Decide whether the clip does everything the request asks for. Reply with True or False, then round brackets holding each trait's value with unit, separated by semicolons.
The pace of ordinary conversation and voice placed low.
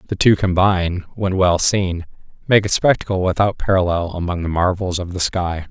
True (180 wpm; 90 Hz)